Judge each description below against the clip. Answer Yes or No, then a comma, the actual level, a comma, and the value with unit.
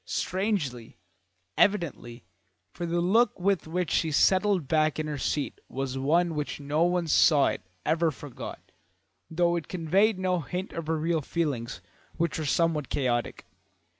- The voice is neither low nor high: Yes, medium, 165 Hz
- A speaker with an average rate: Yes, average, 155 wpm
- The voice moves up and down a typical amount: Yes, average, 3.5 semitones